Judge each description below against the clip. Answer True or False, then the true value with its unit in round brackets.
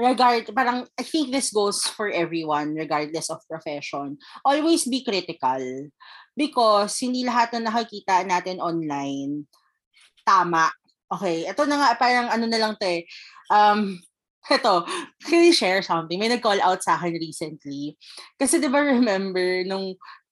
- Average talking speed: True (145 wpm)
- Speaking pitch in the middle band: False (195 Hz)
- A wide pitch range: True (6.9 semitones)